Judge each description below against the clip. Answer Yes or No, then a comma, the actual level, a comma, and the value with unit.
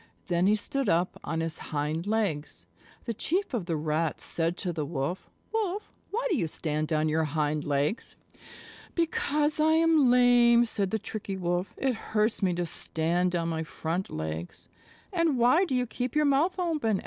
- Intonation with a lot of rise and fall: Yes, wide, 8.5 semitones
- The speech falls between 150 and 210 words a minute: Yes, average, 180 wpm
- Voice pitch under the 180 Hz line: No, high, 195 Hz